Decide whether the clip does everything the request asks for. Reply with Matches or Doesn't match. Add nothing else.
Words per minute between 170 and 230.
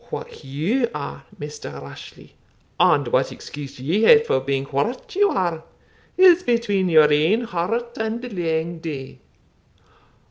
Doesn't match